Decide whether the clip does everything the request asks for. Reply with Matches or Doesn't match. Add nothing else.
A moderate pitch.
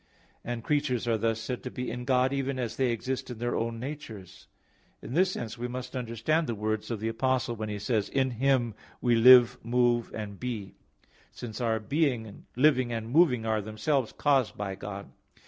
Doesn't match